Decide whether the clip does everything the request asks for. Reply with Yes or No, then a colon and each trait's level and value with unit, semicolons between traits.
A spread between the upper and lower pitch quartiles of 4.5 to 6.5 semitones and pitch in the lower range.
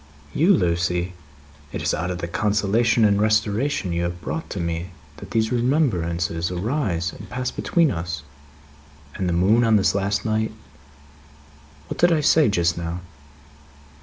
Yes: average, 5.1 semitones; low, 100 Hz